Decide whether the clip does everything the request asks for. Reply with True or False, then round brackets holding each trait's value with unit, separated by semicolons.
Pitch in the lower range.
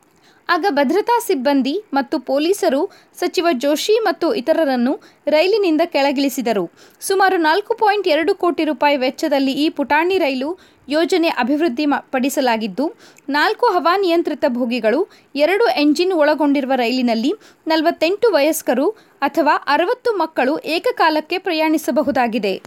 False (315 Hz)